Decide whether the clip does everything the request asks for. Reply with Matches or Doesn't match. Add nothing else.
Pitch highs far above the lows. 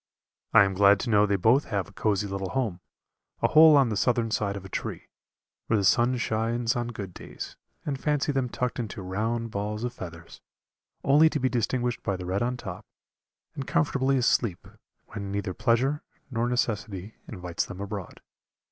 Doesn't match